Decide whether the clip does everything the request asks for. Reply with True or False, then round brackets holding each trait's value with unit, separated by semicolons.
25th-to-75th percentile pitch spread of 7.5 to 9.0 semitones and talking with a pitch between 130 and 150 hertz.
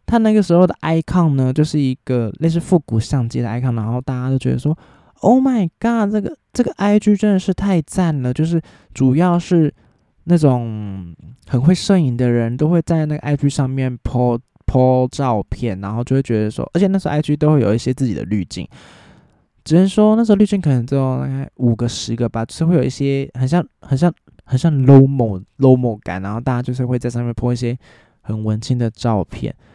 False (5.9 semitones; 135 Hz)